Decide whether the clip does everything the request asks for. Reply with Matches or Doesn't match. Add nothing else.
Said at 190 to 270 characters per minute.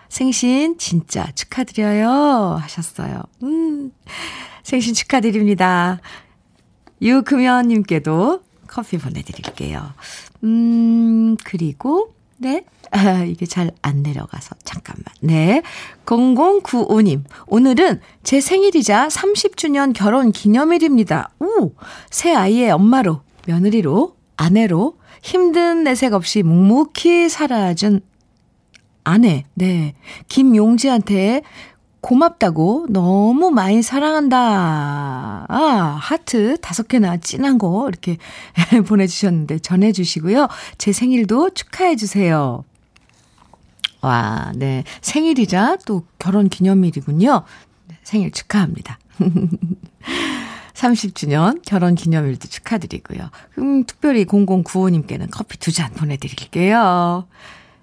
Matches